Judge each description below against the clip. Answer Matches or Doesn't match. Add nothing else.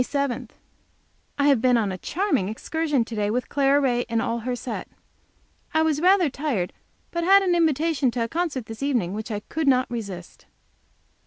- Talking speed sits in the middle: Matches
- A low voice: Doesn't match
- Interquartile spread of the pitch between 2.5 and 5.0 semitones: Doesn't match